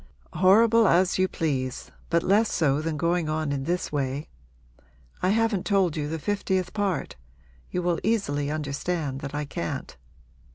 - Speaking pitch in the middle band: Yes, medium, 170 Hz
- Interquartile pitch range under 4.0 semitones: No, average, 4.5 semitones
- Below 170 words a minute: Yes, average, 155 wpm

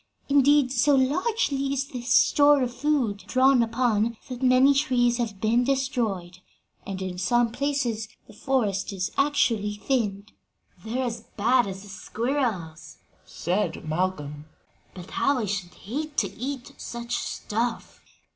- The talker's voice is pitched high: Yes, high, 240 Hz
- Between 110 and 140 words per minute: Yes, slow, 135 wpm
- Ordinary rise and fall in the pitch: Yes, average, 4.8 semitones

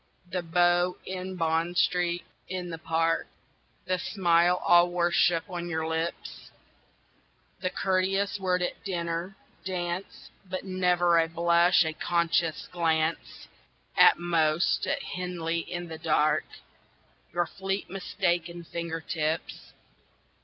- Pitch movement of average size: No, narrow, 1.6 semitones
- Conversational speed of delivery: No, slow, 115 wpm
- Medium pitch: Yes, medium, 175 Hz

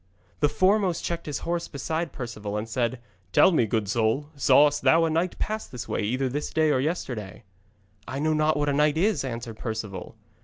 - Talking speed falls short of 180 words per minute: No, average, 195 wpm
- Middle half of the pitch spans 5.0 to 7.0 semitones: Yes, wide, 5.4 semitones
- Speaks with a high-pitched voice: No, medium, 145 Hz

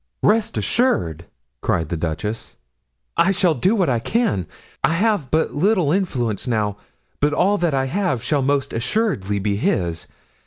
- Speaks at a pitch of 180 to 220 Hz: No, medium, 140 Hz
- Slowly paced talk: No, average, 155 wpm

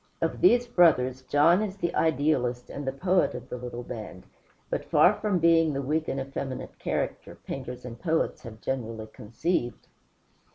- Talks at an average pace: Yes, average, 165 wpm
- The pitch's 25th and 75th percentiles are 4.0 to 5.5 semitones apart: Yes, average, 5.2 semitones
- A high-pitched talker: No, low, 135 Hz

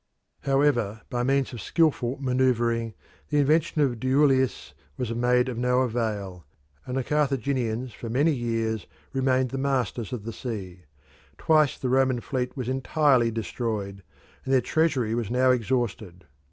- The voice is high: No, low, 125 Hz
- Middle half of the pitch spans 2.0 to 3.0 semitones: Yes, average, 2.7 semitones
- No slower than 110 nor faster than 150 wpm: Yes, average, 145 wpm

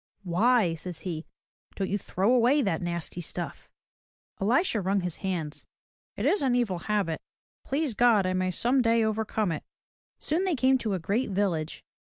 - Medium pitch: No, high, 200 Hz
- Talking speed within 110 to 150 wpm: No, average, 170 wpm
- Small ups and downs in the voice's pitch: No, wide, 5.5 semitones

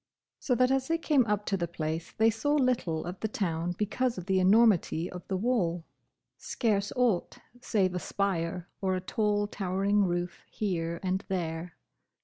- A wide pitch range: No, average, 3.9 semitones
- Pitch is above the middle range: Yes, high, 195 Hz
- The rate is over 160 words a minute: Yes, average, 170 wpm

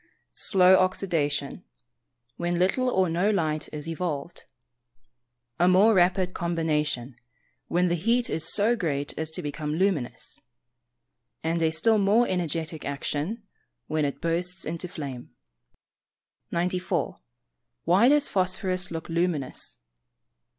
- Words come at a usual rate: No, slow, 115 wpm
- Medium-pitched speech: Yes, medium, 175 Hz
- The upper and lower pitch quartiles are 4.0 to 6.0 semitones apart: No, average, 3.2 semitones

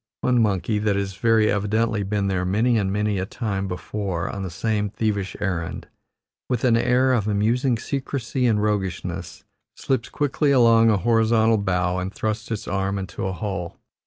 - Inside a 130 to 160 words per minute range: No, average, 170 wpm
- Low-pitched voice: Yes, low, 105 Hz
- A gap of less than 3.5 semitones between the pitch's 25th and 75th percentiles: Yes, average, 2.9 semitones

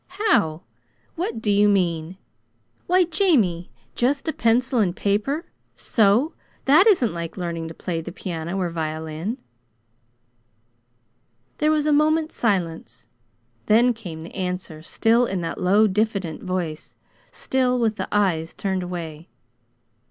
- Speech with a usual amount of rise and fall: No, wide, 6.6 semitones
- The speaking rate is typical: No, slow, 130 wpm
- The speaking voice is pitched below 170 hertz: No, high, 200 Hz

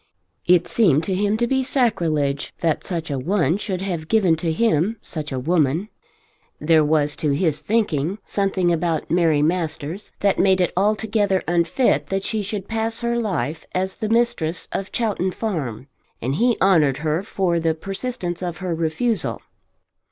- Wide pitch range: No, average, 4.7 semitones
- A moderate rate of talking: Yes, average, 165 wpm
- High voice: No, medium, 180 Hz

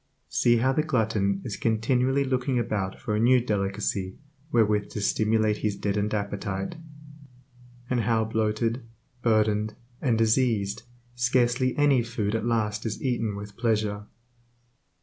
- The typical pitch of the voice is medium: No, low, 110 Hz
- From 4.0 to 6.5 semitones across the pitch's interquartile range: No, narrow, 2.6 semitones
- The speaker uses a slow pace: Yes, slow, 130 wpm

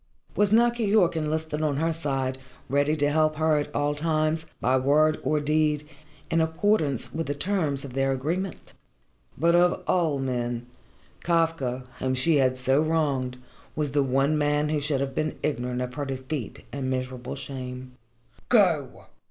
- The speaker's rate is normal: Yes, average, 160 wpm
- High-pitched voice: No, medium, 145 Hz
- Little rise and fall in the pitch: No, average, 3.2 semitones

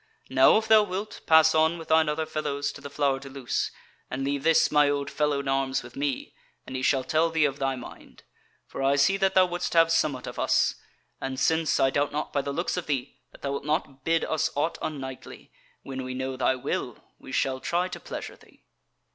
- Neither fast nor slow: No, fast, 225 wpm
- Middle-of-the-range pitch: Yes, medium, 145 Hz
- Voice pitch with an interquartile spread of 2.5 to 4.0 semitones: Yes, average, 3.0 semitones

